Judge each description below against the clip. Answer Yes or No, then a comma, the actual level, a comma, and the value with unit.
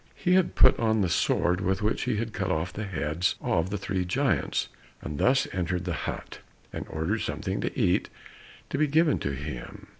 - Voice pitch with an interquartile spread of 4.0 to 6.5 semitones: Yes, average, 4.3 semitones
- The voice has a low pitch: Yes, very low, 95 Hz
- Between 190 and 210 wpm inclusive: Yes, average, 200 wpm